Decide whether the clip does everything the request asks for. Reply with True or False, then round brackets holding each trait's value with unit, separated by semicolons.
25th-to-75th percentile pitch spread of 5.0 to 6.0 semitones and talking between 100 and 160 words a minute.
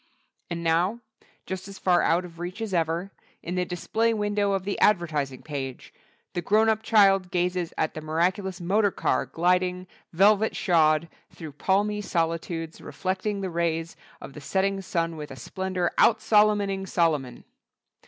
False (3.1 semitones; 155 wpm)